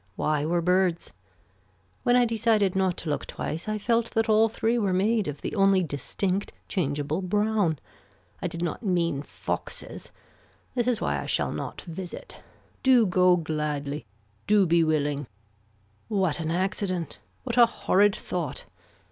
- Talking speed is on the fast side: No, average, 150 wpm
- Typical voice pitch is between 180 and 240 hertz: Yes, medium, 185 Hz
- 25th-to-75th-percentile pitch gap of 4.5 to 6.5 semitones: Yes, average, 4.9 semitones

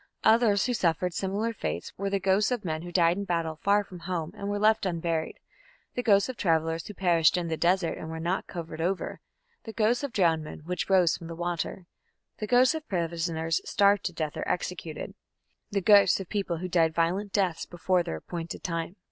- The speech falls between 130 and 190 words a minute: No, fast, 205 wpm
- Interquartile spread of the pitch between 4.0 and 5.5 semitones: No, average, 3.3 semitones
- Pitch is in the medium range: Yes, medium, 180 Hz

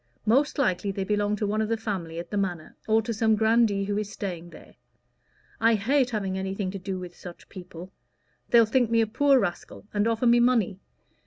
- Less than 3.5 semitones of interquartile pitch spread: Yes, average, 3.1 semitones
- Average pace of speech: No, fast, 210 wpm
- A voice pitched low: No, high, 210 Hz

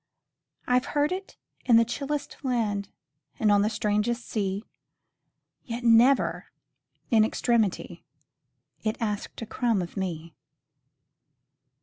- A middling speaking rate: No, slow, 115 wpm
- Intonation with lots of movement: No, average, 3.1 semitones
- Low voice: No, high, 225 Hz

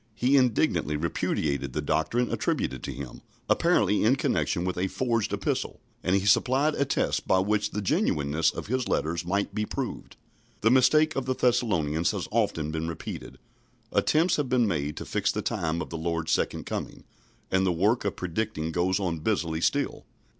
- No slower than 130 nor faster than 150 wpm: No, average, 180 wpm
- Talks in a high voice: No, very low, 95 Hz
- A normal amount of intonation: No, wide, 7.0 semitones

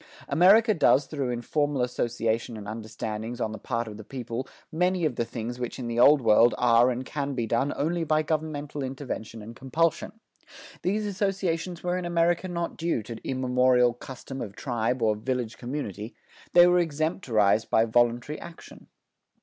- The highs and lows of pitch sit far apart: Yes, wide, 5.8 semitones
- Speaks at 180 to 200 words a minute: No, average, 165 wpm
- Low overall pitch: Yes, low, 130 Hz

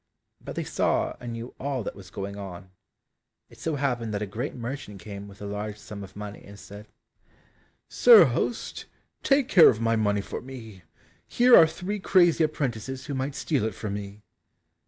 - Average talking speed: Yes, average, 185 wpm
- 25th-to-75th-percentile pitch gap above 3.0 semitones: Yes, wide, 5.6 semitones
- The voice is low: Yes, low, 115 Hz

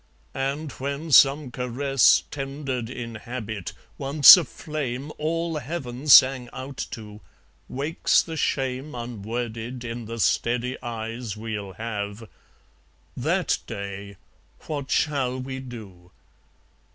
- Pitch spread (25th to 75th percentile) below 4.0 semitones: Yes, average, 3.5 semitones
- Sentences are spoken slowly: Yes, slow, 110 wpm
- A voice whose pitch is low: Yes, low, 125 Hz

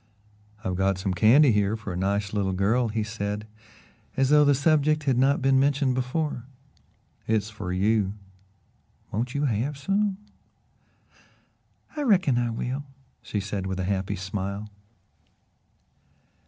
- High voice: No, low, 110 Hz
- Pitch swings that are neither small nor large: No, wide, 5.8 semitones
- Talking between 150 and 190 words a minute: No, average, 140 wpm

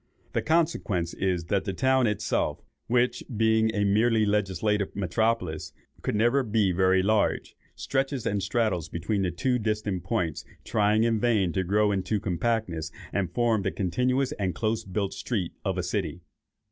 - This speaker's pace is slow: No, average, 160 wpm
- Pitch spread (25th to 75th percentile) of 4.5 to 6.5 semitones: No, average, 3.5 semitones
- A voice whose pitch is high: No, low, 105 Hz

